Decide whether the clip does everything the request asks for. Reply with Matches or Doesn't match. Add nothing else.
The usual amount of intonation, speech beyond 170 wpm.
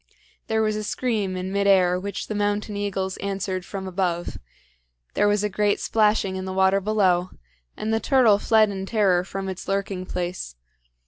Doesn't match